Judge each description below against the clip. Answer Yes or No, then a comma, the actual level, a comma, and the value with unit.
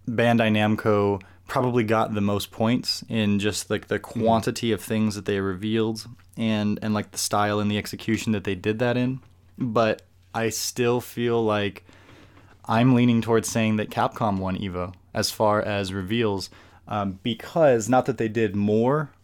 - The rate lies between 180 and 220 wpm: No, average, 170 wpm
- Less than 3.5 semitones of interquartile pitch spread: Yes, narrow, 2.4 semitones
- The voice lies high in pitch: No, low, 105 Hz